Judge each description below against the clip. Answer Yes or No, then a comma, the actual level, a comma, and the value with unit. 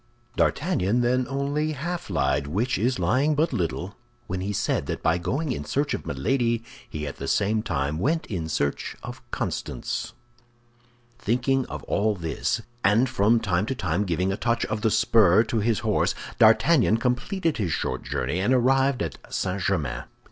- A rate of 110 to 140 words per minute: No, average, 170 wpm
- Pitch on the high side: No, low, 110 Hz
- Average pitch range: No, wide, 6.0 semitones